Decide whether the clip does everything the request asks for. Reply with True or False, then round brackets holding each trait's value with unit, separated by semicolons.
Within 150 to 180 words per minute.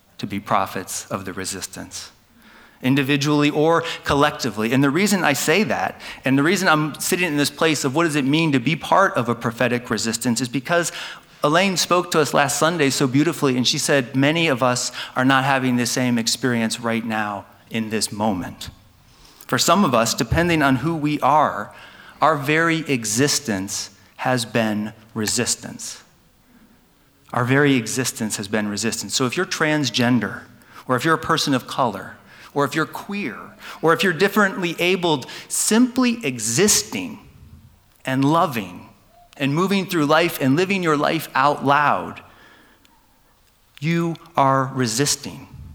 True (155 wpm)